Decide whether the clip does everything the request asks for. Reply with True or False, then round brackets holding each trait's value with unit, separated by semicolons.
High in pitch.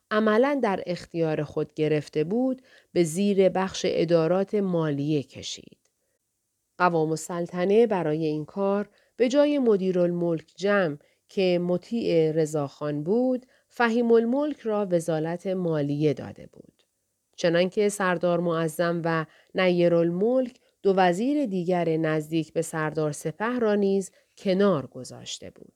False (180 Hz)